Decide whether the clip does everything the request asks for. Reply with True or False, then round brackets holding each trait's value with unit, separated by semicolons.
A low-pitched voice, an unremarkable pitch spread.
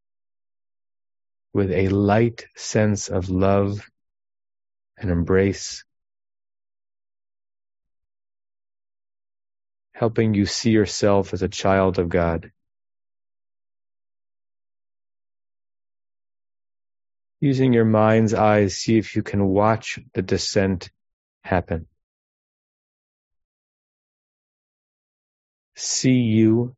False (100 Hz; 0.7 semitones)